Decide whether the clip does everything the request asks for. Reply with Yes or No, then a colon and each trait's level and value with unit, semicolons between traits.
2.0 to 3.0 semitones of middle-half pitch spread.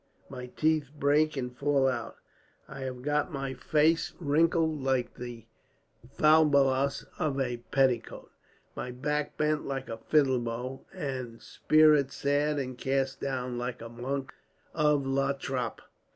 Yes: average, 2.7 semitones